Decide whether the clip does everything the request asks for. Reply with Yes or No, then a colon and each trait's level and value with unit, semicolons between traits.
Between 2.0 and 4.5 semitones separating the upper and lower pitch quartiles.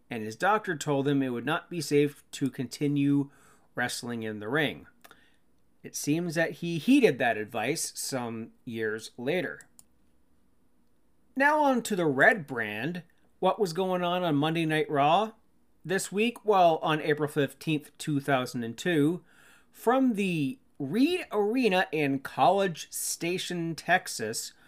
No: average, 5.1 semitones